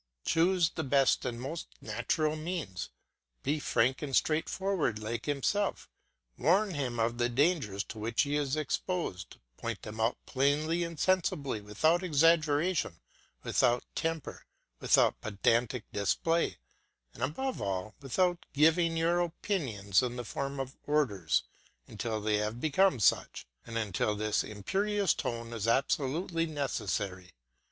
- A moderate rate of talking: No, slow, 130 wpm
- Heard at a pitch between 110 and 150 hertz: Yes, medium, 140 Hz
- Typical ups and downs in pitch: No, wide, 6.5 semitones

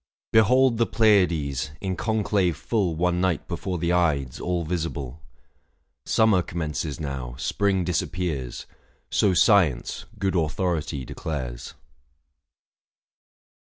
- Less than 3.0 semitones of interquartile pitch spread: No, average, 4.4 semitones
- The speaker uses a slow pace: Yes, slow, 100 wpm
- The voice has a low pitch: Yes, very low, 85 Hz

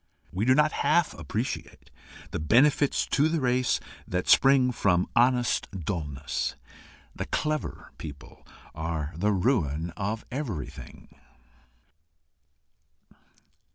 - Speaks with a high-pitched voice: No, low, 105 Hz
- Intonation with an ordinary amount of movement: No, wide, 8.1 semitones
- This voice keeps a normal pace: No, slow, 100 wpm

